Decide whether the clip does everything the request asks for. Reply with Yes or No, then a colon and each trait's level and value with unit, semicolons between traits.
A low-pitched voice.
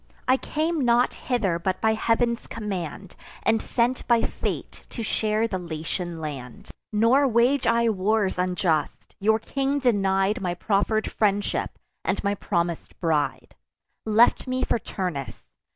No: high, 215 Hz